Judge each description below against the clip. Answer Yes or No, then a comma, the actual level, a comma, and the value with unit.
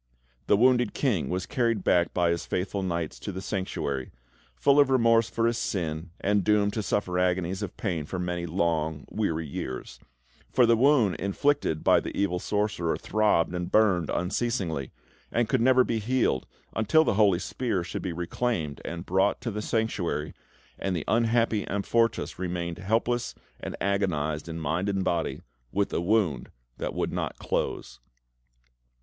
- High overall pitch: No, very low, 95 Hz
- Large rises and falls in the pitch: No, average, 4.8 semitones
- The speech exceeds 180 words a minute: No, average, 165 wpm